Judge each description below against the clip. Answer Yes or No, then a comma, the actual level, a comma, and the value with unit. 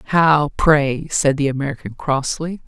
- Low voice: No, medium, 145 Hz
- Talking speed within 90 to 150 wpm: Yes, slow, 135 wpm